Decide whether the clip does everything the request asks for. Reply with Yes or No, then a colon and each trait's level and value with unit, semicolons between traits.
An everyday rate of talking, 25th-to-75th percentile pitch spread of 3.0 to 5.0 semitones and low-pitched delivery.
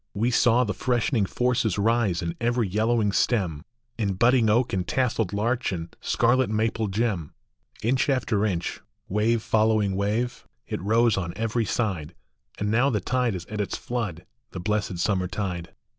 Yes: average, 160 wpm; average, 3.7 semitones; low, 110 Hz